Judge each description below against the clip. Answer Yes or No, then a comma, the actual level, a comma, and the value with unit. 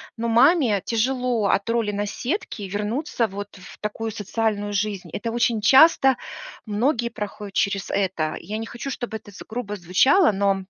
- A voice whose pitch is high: Yes, high, 215 Hz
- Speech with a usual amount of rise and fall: Yes, average, 3.0 semitones